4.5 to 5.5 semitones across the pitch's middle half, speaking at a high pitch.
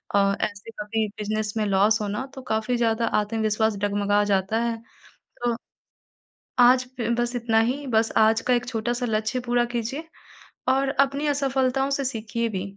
No: average, 2.7 semitones; high, 225 Hz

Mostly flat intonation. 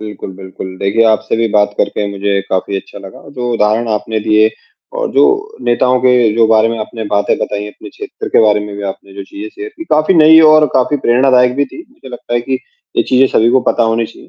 No: average, 3.7 semitones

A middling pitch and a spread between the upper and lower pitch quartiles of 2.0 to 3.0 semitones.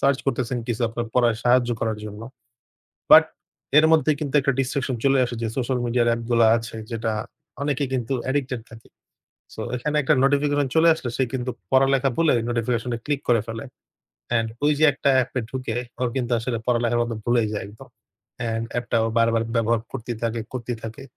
No: low, 120 Hz; average, 2.7 semitones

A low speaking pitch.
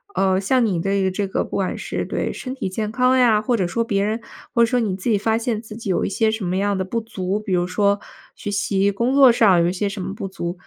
No: high, 205 Hz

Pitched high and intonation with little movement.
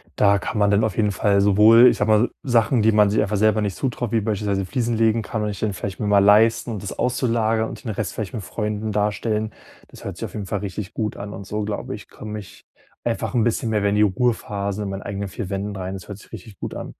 No: low, 105 Hz; narrow, 1.7 semitones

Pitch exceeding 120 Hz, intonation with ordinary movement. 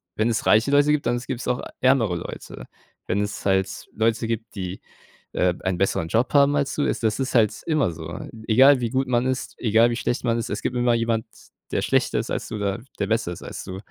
No: low, 115 Hz; average, 3.9 semitones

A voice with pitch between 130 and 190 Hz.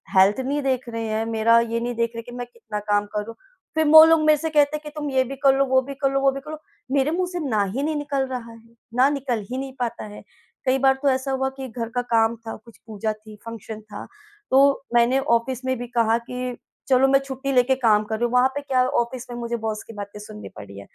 No: very high, 250 Hz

